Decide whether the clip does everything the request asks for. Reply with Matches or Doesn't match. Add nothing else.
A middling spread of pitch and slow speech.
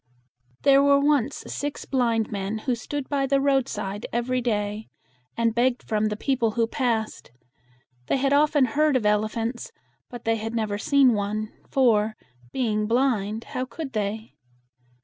Doesn't match